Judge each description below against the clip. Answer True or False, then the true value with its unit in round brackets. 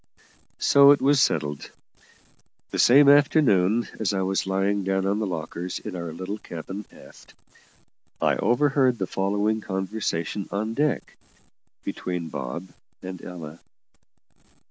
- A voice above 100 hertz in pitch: False (95 Hz)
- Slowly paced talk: True (125 wpm)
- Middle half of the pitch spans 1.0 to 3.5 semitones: False (3.9 semitones)